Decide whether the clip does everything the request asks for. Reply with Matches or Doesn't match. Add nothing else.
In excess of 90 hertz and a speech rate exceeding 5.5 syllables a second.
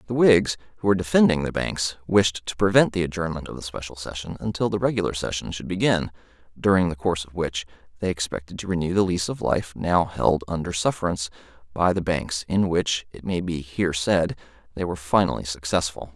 Doesn't match